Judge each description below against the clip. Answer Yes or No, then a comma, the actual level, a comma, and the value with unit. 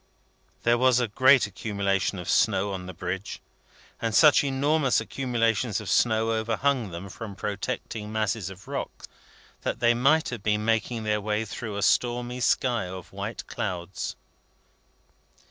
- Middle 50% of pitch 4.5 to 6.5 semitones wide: No, average, 3.5 semitones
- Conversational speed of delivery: Yes, average, 145 wpm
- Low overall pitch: Yes, low, 110 Hz